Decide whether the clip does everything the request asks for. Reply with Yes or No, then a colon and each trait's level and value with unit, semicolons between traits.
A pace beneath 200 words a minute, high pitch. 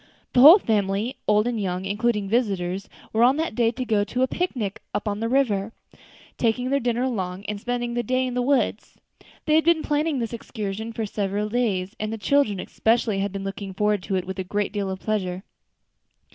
No: fast, 205 wpm; high, 215 Hz